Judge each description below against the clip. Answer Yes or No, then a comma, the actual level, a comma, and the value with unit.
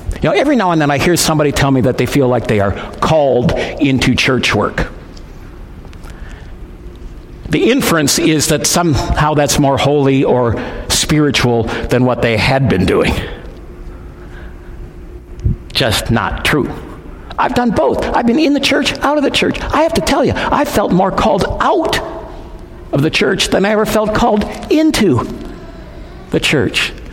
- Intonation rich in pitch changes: Yes, wide, 9.0 semitones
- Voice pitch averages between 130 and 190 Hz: Yes, low, 135 Hz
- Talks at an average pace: Yes, average, 160 wpm